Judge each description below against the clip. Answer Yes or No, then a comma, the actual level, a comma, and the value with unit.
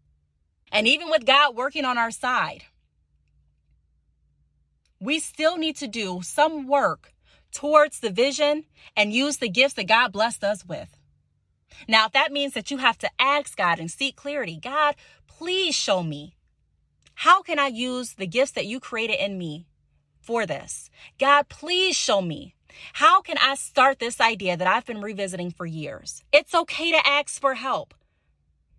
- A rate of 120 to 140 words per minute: No, average, 165 wpm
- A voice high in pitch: Yes, high, 235 Hz